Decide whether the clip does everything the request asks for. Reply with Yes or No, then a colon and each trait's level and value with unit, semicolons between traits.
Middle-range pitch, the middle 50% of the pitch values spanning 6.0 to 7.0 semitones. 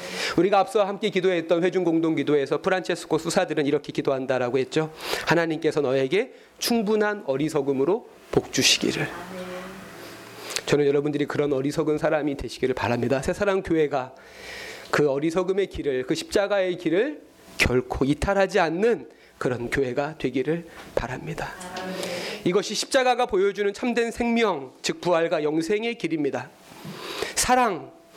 No: medium, 170 Hz; wide, 5.4 semitones